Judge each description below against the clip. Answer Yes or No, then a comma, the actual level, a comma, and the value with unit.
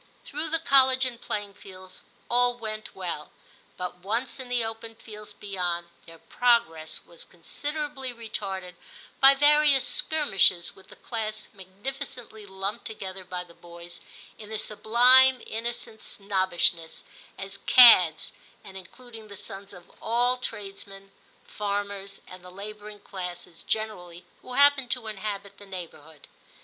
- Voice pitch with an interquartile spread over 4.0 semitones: Yes, average, 4.5 semitones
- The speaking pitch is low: No, high, 205 Hz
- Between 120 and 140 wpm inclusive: Yes, slow, 135 wpm